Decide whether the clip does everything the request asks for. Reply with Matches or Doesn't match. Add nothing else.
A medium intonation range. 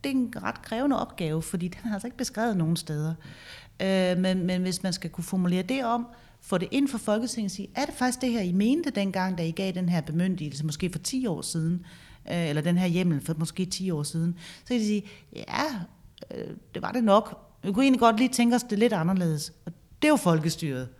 Doesn't match